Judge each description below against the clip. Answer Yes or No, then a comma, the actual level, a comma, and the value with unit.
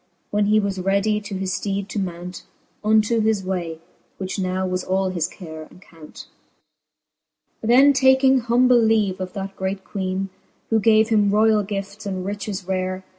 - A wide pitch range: No, narrow, 2.6 semitones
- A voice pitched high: Yes, high, 195 Hz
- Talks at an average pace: Yes, average, 170 wpm